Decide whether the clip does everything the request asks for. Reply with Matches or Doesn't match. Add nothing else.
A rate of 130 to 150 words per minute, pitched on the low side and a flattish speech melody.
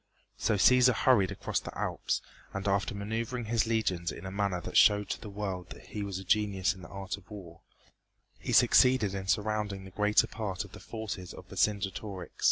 Doesn't match